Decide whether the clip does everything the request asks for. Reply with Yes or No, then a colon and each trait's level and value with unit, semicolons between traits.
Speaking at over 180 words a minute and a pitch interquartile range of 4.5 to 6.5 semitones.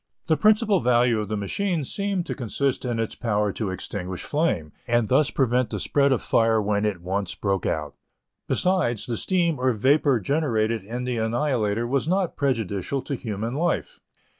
No: average, 175 wpm; wide, 5.4 semitones